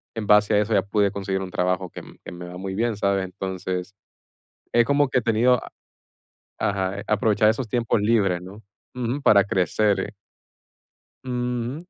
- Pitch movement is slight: No, average, 3.4 semitones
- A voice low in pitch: Yes, low, 105 Hz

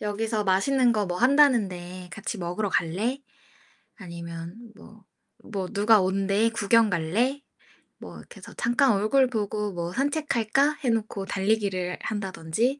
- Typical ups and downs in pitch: Yes, average, 4.1 semitones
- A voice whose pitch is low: No, high, 210 Hz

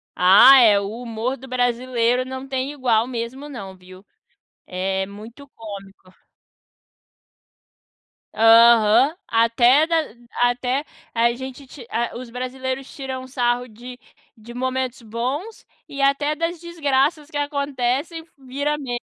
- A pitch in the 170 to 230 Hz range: No, very high, 250 Hz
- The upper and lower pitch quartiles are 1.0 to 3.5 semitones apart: Yes, average, 3.0 semitones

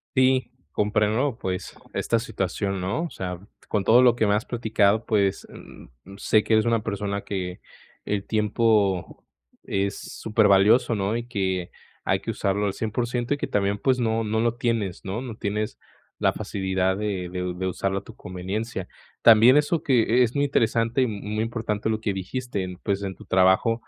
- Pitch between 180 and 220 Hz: No, low, 105 Hz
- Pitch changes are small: No, average, 3.0 semitones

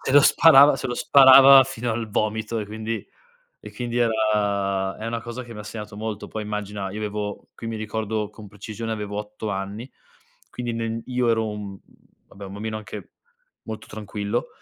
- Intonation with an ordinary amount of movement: No, narrow, 2.0 semitones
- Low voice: Yes, low, 110 Hz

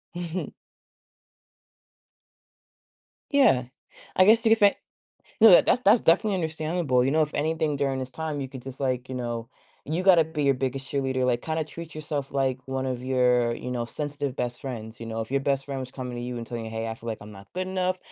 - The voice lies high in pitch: No, low, 135 Hz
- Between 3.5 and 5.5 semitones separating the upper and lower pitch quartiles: Yes, average, 4.3 semitones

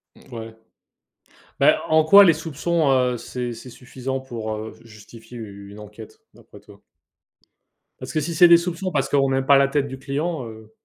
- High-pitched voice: No, low, 135 Hz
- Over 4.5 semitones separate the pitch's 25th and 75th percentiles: Yes, wide, 5.6 semitones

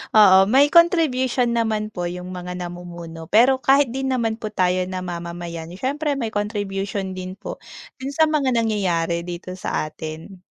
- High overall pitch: Yes, high, 200 Hz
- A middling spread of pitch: No, wide, 6.2 semitones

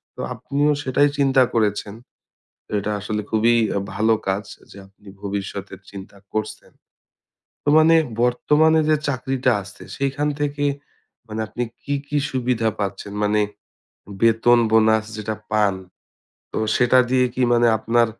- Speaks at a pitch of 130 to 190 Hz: No, low, 115 Hz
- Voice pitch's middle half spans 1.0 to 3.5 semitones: No, average, 4.1 semitones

